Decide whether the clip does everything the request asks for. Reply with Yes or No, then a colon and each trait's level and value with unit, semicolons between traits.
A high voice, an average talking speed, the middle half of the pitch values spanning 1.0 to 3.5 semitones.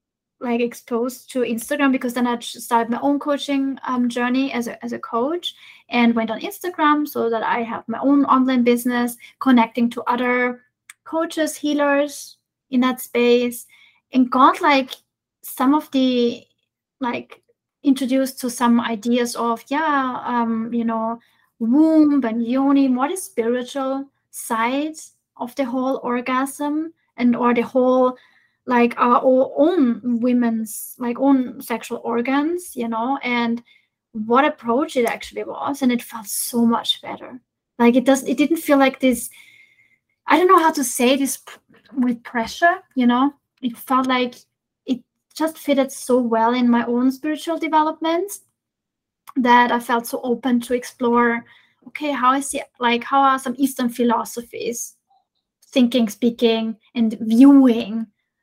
Yes: very high, 255 Hz; average, 150 wpm; average, 2.8 semitones